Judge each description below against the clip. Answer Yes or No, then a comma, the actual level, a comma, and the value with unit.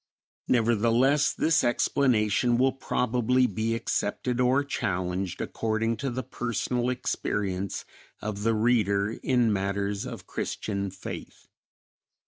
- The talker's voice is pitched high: No, low, 115 Hz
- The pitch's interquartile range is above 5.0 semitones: No, average, 3.6 semitones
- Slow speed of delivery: Yes, slow, 110 wpm